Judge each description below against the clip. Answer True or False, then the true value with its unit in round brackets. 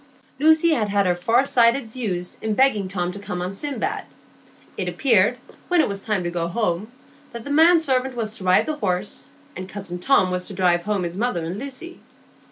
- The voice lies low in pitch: False (210 Hz)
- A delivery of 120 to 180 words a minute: False (205 wpm)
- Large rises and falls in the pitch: True (6.2 semitones)